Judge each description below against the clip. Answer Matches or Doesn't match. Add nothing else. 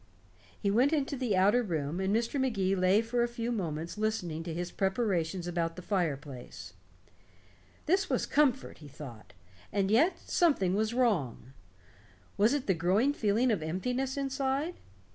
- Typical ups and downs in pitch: Doesn't match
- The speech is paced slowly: Doesn't match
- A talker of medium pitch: Doesn't match